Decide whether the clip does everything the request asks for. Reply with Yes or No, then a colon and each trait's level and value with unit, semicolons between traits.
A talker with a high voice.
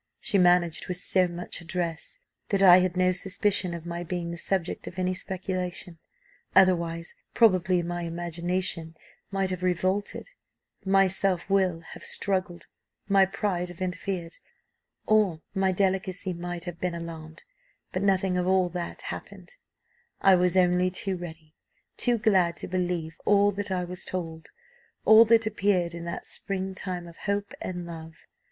No: medium, 180 Hz